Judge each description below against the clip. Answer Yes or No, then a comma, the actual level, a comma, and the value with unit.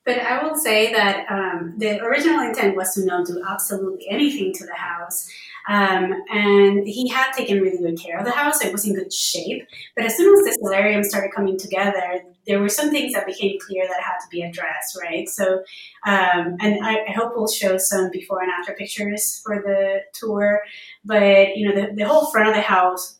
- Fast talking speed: Yes, fast, 215 wpm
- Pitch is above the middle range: Yes, high, 200 Hz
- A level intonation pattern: Yes, narrow, 2.0 semitones